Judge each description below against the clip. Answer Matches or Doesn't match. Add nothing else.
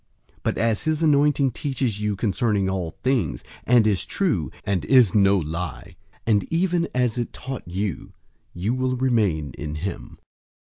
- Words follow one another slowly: Doesn't match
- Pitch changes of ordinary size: Doesn't match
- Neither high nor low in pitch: Doesn't match